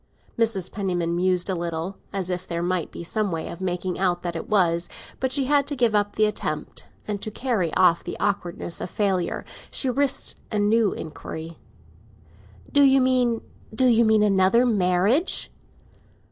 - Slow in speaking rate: No, average, 170 wpm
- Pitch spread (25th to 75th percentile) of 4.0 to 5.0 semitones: Yes, average, 4.6 semitones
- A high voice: Yes, high, 195 Hz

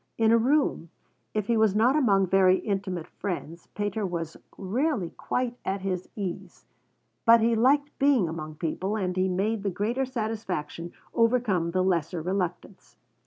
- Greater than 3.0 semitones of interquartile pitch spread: Yes, average, 4.1 semitones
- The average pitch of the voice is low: No, high, 195 Hz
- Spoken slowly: No, average, 155 wpm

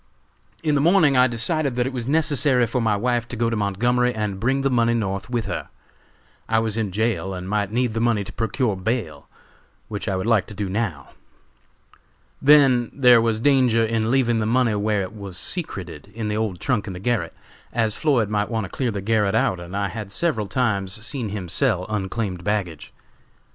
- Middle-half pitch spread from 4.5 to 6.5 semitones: No, average, 3.6 semitones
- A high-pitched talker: No, low, 110 Hz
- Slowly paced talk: No, fast, 205 wpm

